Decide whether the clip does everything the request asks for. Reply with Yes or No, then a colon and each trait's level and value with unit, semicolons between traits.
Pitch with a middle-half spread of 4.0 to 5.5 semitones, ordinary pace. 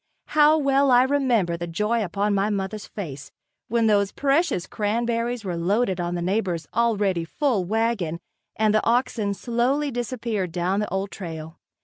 Yes: average, 4.5 semitones; average, 155 wpm